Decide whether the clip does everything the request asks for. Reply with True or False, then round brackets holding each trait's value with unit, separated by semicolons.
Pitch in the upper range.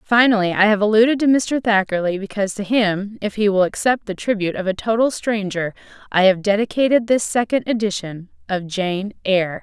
True (205 Hz)